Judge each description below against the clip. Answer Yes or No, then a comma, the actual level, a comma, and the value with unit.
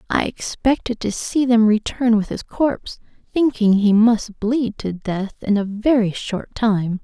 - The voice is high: Yes, high, 220 Hz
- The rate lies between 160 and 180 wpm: Yes, average, 170 wpm